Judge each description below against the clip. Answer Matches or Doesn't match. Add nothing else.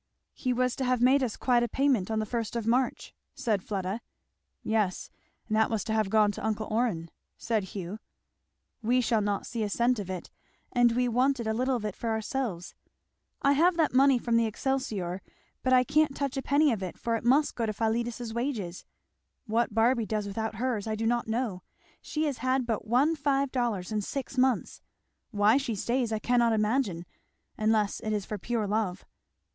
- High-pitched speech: Matches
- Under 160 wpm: Doesn't match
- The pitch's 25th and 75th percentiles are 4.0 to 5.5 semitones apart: Doesn't match